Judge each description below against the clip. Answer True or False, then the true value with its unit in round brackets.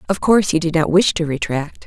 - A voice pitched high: False (170 Hz)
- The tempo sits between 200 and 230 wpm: False (260 wpm)